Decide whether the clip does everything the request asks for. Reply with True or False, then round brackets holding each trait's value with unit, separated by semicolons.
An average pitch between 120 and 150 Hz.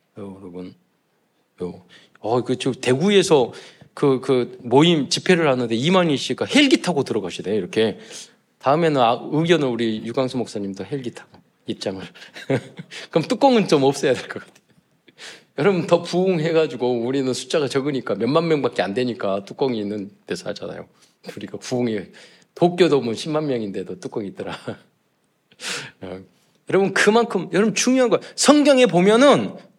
True (135 Hz)